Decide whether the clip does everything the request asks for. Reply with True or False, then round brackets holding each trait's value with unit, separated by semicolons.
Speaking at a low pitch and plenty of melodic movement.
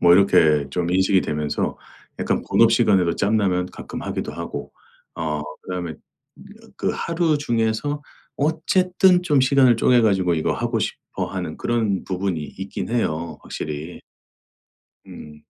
True (100 Hz; 6.8 semitones)